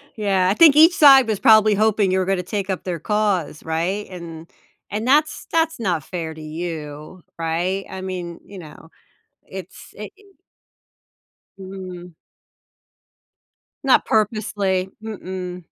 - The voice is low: No, high, 190 Hz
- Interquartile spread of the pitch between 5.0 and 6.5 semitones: No, average, 3.6 semitones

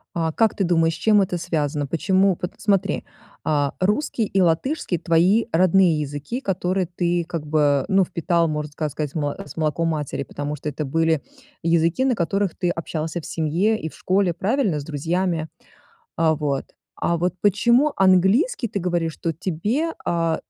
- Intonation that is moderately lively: Yes, average, 3.5 semitones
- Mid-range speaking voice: Yes, medium, 170 Hz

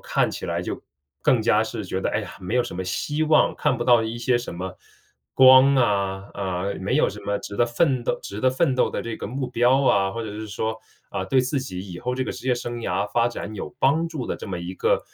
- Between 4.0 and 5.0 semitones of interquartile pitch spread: Yes, average, 4.4 semitones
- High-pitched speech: No, low, 120 Hz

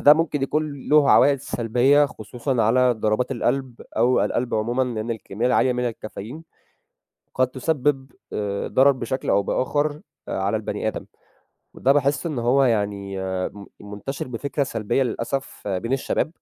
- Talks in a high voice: No, low, 125 Hz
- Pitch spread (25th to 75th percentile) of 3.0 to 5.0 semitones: Yes, average, 3.5 semitones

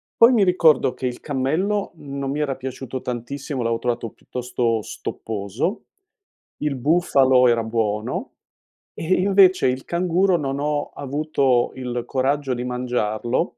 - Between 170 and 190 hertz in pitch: No, low, 130 Hz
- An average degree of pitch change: Yes, average, 4.0 semitones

